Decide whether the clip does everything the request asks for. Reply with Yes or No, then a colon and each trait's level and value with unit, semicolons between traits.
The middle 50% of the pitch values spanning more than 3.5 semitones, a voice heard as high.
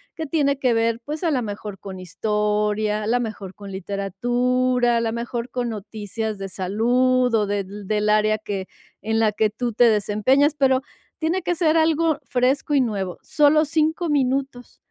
Yes: average, 4.3 semitones; high, 230 Hz